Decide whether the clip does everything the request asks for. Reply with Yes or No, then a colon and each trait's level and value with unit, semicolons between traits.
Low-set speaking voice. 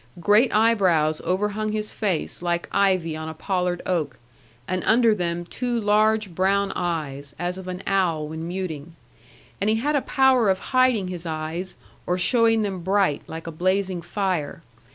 No: medium, 185 Hz